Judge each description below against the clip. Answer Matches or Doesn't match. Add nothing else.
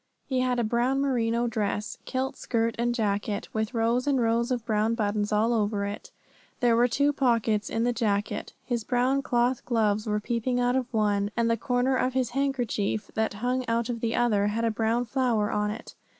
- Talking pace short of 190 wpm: Doesn't match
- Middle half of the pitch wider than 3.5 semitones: Doesn't match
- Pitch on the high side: Matches